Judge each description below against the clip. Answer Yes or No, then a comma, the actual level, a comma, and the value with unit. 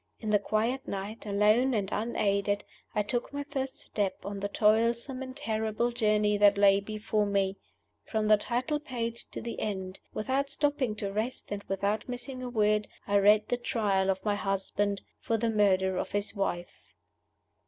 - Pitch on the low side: No, high, 215 Hz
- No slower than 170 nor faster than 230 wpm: Yes, average, 175 wpm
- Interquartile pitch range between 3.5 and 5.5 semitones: No, average, 2.9 semitones